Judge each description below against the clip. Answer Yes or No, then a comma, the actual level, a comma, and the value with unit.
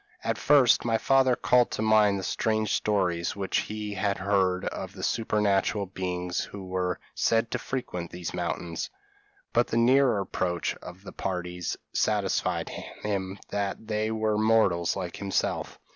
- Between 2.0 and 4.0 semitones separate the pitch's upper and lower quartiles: Yes, average, 3.0 semitones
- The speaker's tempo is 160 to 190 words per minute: No, average, 150 wpm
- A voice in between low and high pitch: No, low, 100 Hz